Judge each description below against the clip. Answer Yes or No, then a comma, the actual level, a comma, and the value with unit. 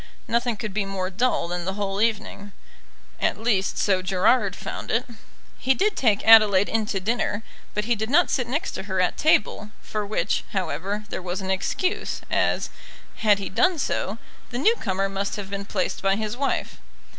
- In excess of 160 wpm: Yes, average, 190 wpm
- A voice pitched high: Yes, high, 210 Hz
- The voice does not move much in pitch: No, average, 3.0 semitones